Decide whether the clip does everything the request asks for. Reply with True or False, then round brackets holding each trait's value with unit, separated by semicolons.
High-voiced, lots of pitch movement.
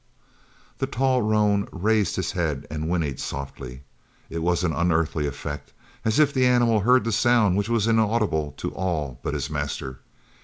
False (95 Hz; 6.6 semitones)